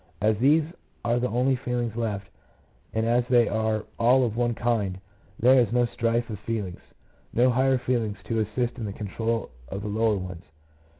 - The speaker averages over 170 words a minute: Yes, average, 180 wpm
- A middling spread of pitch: No, narrow, 2.3 semitones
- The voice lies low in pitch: Yes, low, 115 Hz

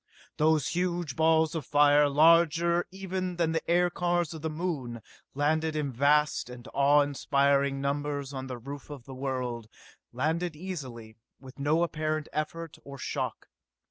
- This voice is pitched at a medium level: Yes, medium, 150 Hz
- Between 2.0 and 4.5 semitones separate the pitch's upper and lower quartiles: Yes, average, 3.1 semitones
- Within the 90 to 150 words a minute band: Yes, average, 145 wpm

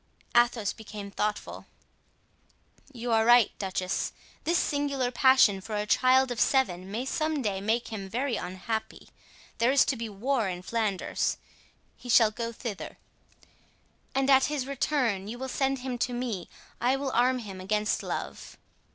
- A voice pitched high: Yes, high, 235 Hz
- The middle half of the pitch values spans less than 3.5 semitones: No, average, 4.0 semitones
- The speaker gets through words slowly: No, average, 155 wpm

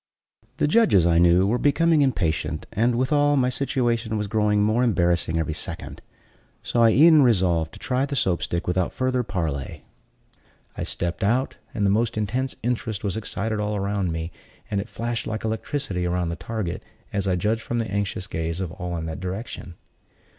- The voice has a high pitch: No, low, 105 Hz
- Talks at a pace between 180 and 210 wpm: Yes, average, 185 wpm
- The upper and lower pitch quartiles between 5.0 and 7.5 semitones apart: Yes, average, 5.3 semitones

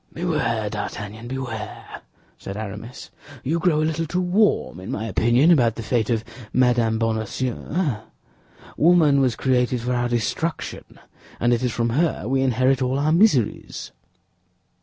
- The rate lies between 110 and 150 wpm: Yes, average, 145 wpm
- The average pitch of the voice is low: Yes, low, 125 Hz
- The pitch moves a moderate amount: Yes, average, 4.9 semitones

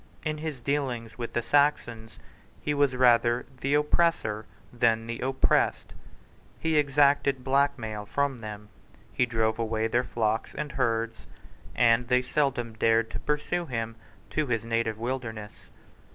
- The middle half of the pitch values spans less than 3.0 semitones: No, average, 3.8 semitones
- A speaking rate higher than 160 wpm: No, average, 140 wpm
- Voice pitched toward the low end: Yes, low, 120 Hz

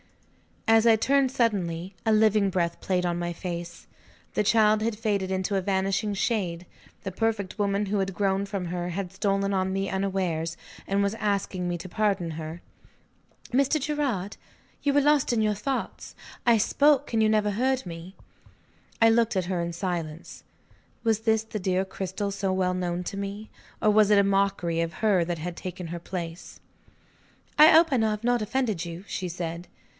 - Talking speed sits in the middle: Yes, average, 180 wpm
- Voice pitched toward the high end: Yes, high, 195 Hz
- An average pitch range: Yes, average, 3.4 semitones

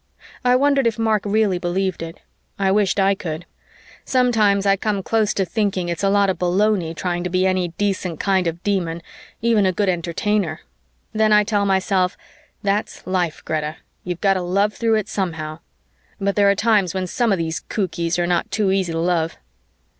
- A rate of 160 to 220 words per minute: Yes, average, 190 wpm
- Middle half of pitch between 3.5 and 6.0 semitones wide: No, average, 3.0 semitones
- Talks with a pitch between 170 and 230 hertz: Yes, high, 190 Hz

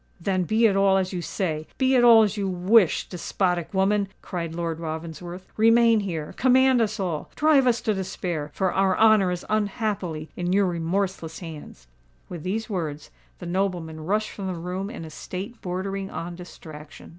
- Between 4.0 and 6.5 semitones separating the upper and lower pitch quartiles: No, average, 3.6 semitones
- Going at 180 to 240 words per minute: No, average, 165 wpm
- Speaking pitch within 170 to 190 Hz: Yes, medium, 185 Hz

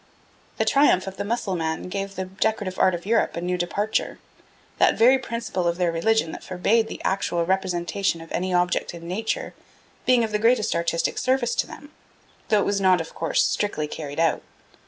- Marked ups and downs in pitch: No, average, 4.2 semitones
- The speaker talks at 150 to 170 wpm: No, average, 190 wpm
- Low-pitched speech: No, high, 190 Hz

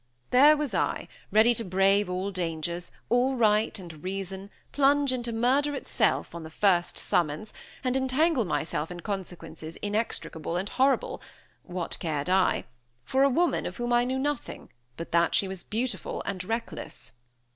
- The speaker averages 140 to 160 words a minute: Yes, average, 155 wpm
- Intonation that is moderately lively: No, wide, 6.3 semitones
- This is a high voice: Yes, high, 205 Hz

